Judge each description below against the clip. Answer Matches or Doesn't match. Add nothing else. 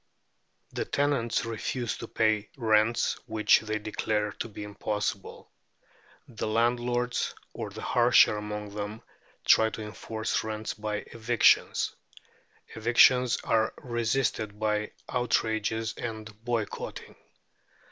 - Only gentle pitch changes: Matches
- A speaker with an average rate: Doesn't match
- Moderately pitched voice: Doesn't match